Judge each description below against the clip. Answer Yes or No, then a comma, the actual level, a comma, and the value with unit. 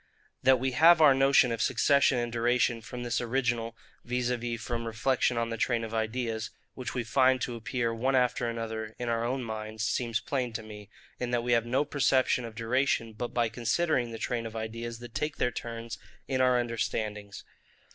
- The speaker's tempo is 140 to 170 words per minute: No, average, 195 wpm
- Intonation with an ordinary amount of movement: No, narrow, 1.9 semitones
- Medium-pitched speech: No, low, 120 Hz